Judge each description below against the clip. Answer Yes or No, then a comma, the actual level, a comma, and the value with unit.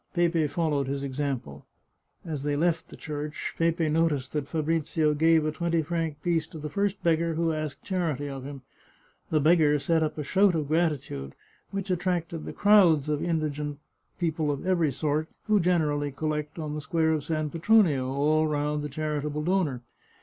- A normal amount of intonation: No, narrow, 2.3 semitones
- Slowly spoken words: No, average, 175 wpm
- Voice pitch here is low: No, medium, 155 Hz